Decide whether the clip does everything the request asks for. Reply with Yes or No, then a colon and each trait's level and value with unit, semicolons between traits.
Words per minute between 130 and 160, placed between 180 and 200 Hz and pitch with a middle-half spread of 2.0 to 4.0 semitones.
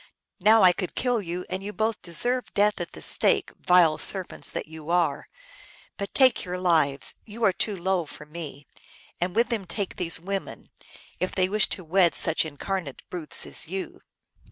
No: average, 185 wpm; medium, 185 Hz; average, 3.3 semitones